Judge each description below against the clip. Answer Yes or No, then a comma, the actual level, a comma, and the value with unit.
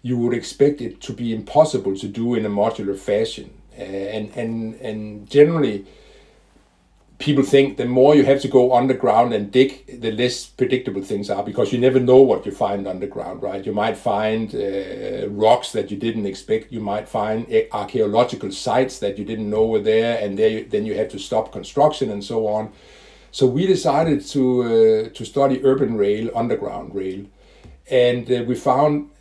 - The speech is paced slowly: No, average, 180 wpm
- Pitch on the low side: Yes, low, 115 Hz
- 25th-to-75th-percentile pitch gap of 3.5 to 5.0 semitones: Yes, average, 4.1 semitones